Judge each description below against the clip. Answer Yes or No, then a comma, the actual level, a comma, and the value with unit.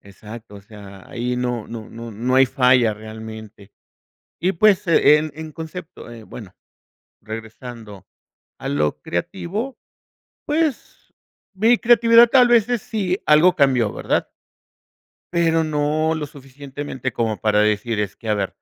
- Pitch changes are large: Yes, wide, 7.6 semitones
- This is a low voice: Yes, low, 130 Hz